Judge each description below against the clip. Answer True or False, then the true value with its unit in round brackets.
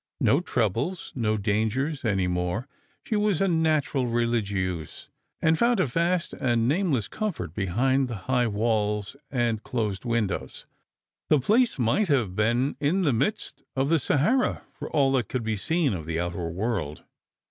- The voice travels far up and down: True (6.4 semitones)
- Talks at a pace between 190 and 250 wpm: False (160 wpm)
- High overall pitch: False (120 Hz)